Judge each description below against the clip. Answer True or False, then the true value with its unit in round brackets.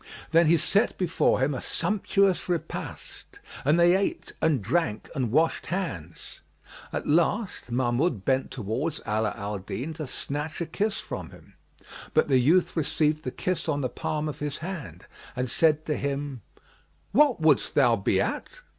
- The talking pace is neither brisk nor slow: True (165 wpm)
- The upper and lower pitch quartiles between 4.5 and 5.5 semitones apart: True (4.8 semitones)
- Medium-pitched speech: True (150 Hz)